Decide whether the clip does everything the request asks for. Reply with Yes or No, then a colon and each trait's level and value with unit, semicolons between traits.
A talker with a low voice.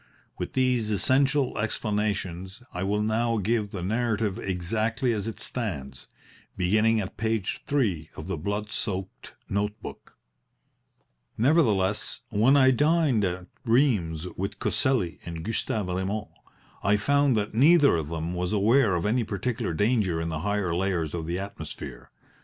Yes: low, 105 Hz